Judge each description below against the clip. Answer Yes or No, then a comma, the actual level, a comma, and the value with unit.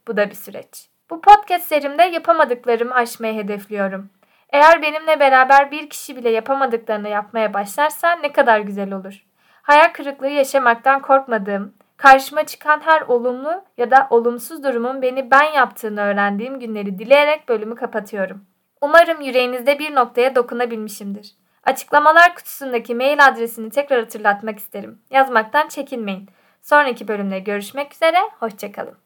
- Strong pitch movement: No, average, 5.0 semitones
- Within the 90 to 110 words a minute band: No, average, 130 wpm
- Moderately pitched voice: No, very high, 250 Hz